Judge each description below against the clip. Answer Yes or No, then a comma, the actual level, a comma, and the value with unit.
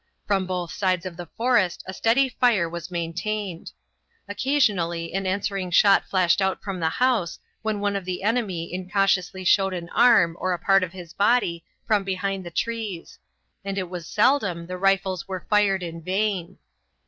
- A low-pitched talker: No, high, 190 Hz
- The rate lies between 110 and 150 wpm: No, average, 170 wpm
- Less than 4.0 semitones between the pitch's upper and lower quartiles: Yes, average, 2.7 semitones